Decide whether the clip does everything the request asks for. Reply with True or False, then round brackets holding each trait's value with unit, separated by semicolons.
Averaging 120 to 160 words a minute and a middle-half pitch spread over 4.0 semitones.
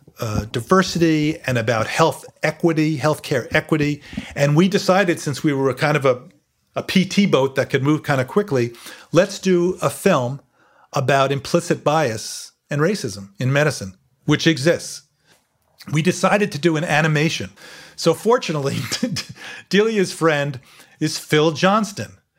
False (140 wpm; 3.7 semitones)